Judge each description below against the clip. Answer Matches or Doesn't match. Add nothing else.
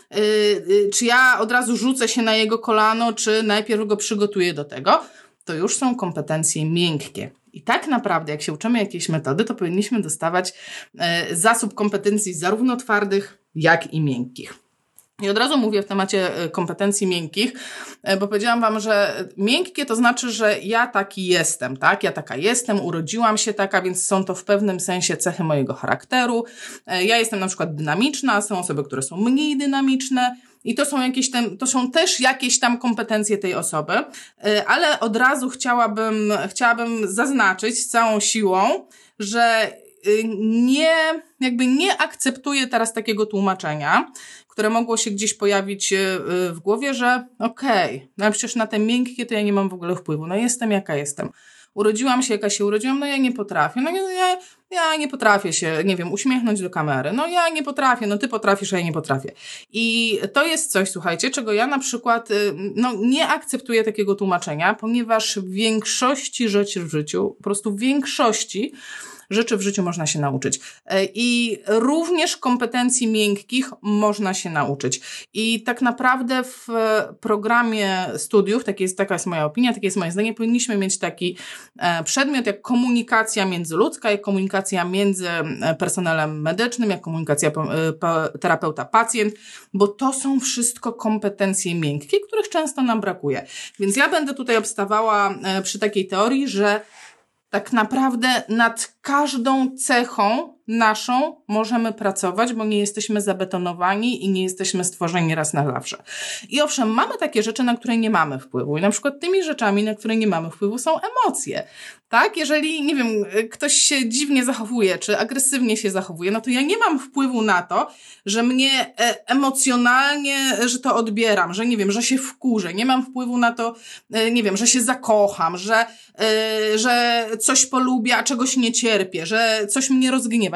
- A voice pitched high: Matches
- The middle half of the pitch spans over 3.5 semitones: Matches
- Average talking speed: Doesn't match